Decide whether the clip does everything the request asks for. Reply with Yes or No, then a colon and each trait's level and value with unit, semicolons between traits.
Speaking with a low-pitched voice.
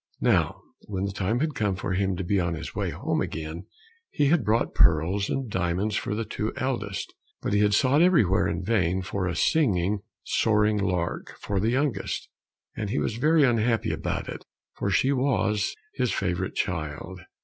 Yes: low, 100 Hz